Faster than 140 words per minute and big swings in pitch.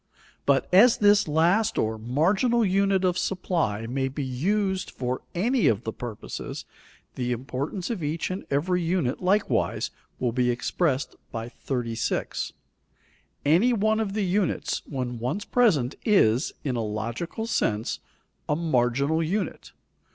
No: slow, 135 wpm; wide, 8.0 semitones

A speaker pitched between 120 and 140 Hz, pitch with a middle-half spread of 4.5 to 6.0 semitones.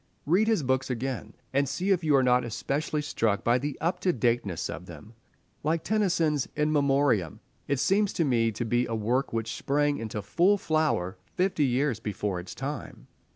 Yes: low, 135 Hz; average, 5.3 semitones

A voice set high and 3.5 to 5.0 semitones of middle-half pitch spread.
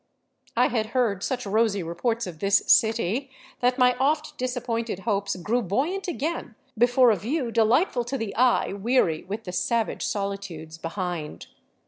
Yes: high, 225 Hz; average, 4.1 semitones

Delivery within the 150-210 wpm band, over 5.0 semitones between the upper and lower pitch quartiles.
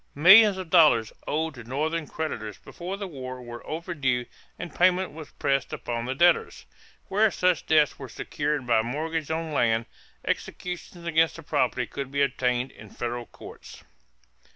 Yes: average, 155 wpm; wide, 5.4 semitones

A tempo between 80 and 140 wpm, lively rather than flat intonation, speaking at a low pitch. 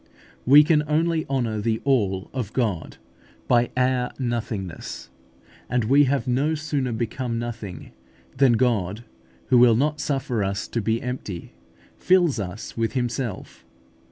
No: slow, 135 wpm; average, 3.6 semitones; low, 120 Hz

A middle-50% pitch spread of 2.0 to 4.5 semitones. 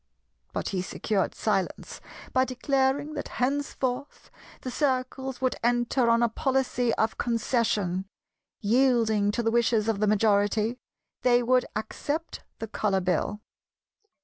Yes: average, 3.3 semitones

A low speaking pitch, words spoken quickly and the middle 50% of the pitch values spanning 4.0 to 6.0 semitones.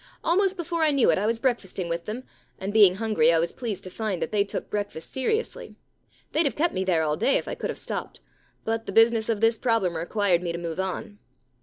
No: high, 210 Hz; fast, 235 wpm; average, 4.5 semitones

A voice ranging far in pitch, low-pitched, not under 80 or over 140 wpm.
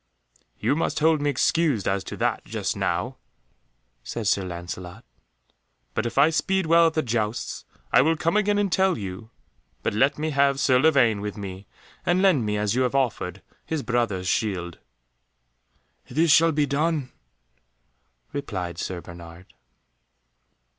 No: wide, 8.1 semitones; low, 125 Hz; average, 155 wpm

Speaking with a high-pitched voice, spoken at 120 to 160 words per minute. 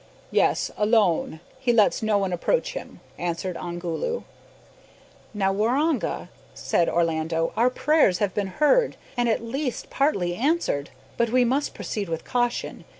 Yes: high, 215 Hz; average, 140 wpm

